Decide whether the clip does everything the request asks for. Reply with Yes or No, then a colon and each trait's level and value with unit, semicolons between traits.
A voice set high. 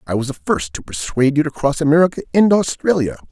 No: medium, 140 Hz